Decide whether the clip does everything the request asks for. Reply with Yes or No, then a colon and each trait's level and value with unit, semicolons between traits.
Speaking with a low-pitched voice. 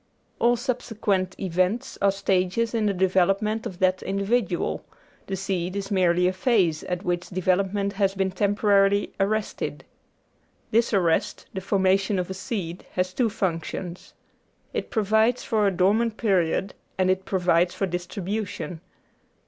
No: high, 195 Hz